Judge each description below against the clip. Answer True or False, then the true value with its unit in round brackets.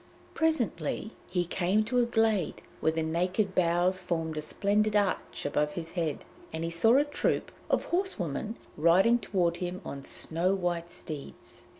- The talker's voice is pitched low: False (180 Hz)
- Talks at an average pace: True (160 wpm)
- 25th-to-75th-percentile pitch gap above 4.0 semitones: True (4.4 semitones)